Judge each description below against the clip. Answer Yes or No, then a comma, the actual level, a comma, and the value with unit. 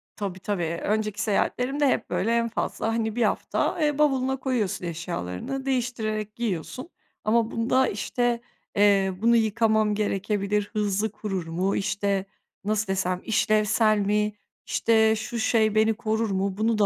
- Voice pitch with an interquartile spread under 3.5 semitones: Yes, narrow, 2.5 semitones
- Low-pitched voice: No, high, 215 Hz